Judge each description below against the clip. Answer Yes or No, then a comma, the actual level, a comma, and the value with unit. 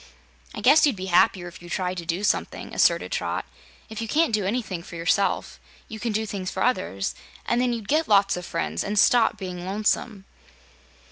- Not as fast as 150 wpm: No, average, 200 wpm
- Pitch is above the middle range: Yes, high, 200 Hz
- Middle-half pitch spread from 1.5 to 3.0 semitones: No, average, 4.0 semitones